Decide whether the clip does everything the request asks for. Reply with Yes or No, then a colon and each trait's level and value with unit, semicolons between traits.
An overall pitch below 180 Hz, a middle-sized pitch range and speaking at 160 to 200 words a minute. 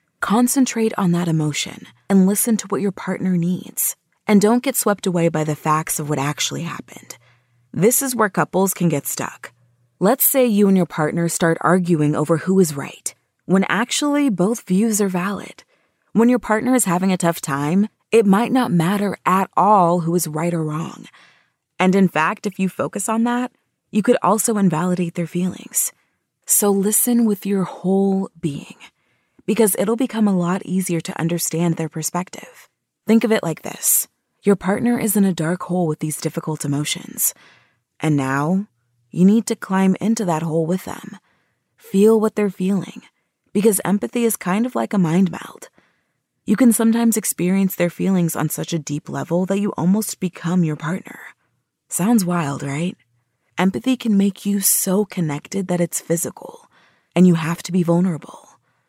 No: medium, 185 Hz; average, 4.1 semitones; average, 175 wpm